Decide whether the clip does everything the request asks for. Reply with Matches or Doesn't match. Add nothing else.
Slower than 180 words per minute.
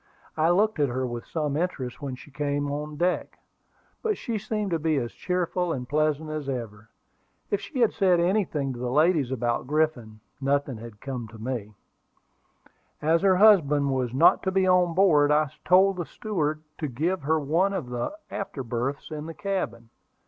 Doesn't match